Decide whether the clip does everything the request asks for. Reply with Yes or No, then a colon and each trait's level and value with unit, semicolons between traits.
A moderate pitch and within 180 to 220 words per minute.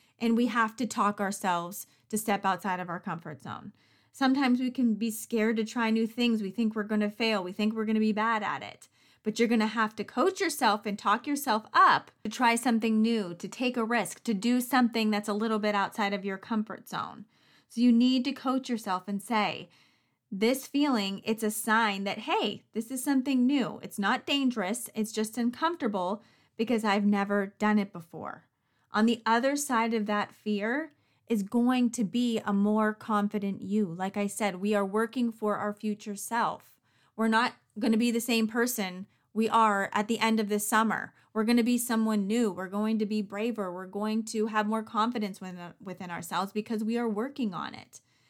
No: high, 220 Hz; fast, 205 wpm